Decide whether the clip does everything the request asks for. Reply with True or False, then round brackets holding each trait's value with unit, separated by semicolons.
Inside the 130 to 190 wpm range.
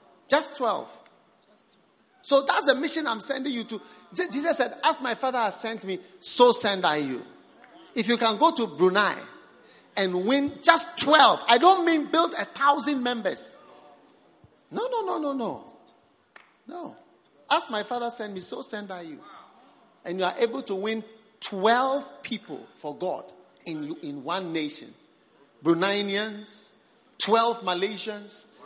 True (150 wpm)